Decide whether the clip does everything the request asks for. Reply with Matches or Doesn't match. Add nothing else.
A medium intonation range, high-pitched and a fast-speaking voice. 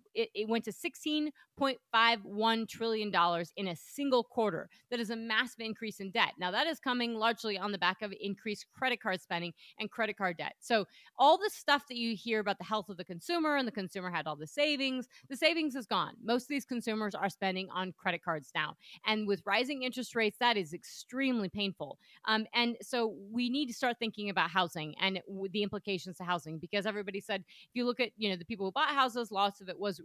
Matches